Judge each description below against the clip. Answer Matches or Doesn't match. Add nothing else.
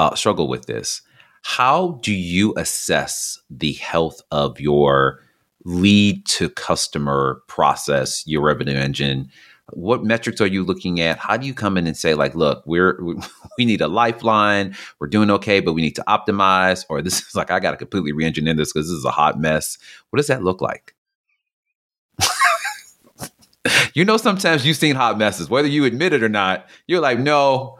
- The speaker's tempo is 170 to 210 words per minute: Matches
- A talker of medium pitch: Doesn't match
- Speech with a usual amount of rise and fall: Doesn't match